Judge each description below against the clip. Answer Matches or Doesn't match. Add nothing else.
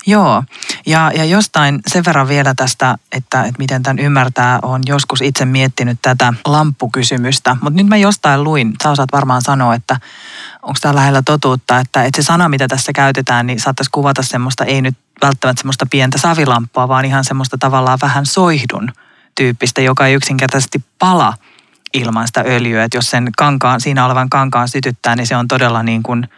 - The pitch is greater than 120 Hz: Matches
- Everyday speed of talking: Doesn't match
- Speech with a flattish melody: Matches